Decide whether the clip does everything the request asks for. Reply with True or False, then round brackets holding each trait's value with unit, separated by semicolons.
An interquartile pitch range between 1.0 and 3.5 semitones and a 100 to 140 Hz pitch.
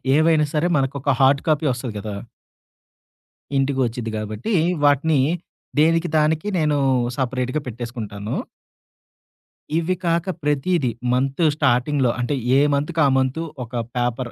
False (3.9 semitones; 135 Hz)